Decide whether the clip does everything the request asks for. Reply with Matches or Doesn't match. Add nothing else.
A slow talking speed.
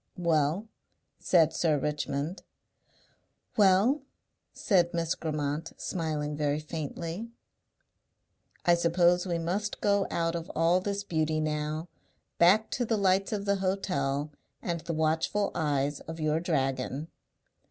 Matches